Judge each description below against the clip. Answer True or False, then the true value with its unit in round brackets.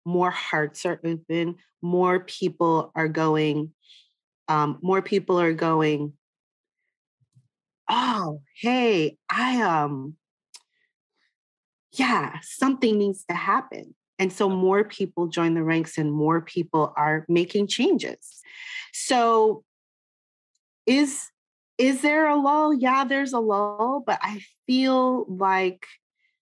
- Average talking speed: False (110 wpm)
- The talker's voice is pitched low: False (190 Hz)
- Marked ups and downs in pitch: True (7.7 semitones)